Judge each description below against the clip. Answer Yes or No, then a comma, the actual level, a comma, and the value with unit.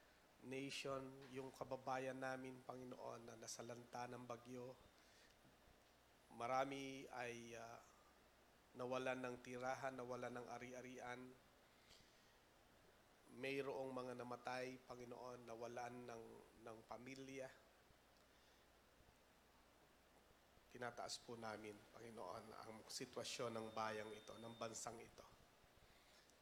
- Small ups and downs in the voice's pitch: Yes, narrow, 2.1 semitones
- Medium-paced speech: No, slow, 85 wpm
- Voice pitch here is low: Yes, low, 125 Hz